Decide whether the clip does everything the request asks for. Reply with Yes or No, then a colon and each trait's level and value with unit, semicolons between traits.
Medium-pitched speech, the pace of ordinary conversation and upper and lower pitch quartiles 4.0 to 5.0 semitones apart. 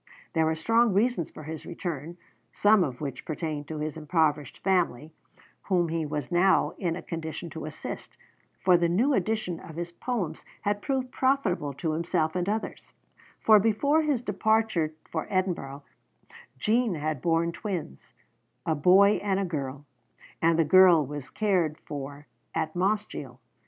Yes: medium, 170 Hz; average, 155 wpm; average, 4.6 semitones